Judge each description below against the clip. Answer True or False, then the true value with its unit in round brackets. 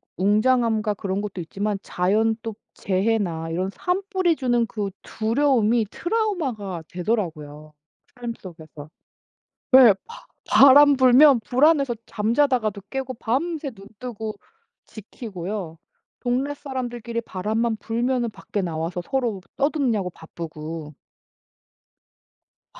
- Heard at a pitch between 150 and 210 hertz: False (225 Hz)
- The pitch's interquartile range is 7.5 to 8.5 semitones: False (5.3 semitones)